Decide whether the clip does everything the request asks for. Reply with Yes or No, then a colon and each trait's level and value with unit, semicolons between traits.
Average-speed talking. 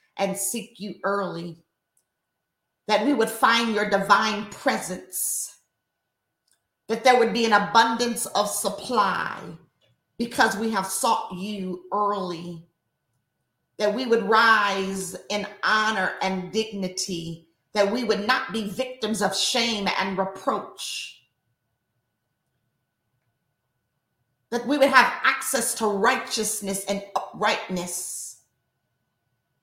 No: slow, 105 wpm